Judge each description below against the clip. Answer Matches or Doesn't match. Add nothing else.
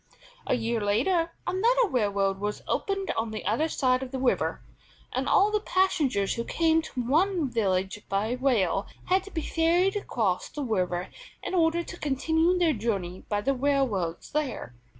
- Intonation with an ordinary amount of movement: Doesn't match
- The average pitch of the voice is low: Doesn't match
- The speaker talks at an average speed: Matches